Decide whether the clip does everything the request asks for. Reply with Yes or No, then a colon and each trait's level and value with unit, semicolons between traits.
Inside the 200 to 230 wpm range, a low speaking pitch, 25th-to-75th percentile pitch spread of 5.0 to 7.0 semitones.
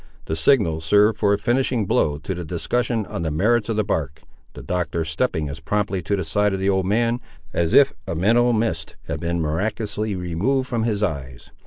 Yes: fast, 205 wpm; very low, 95 Hz; wide, 5.4 semitones